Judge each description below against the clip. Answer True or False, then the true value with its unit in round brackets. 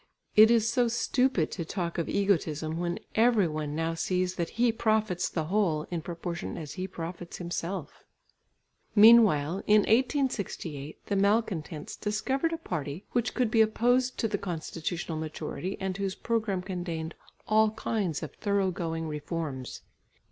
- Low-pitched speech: False (185 Hz)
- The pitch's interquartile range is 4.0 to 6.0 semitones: True (5.0 semitones)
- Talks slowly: False (150 wpm)